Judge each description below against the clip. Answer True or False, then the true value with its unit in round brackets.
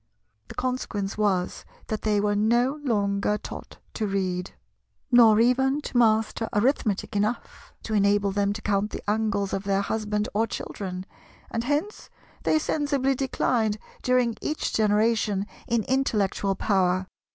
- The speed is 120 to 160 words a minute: True (140 wpm)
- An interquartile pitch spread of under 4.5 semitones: True (3.3 semitones)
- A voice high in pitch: True (215 Hz)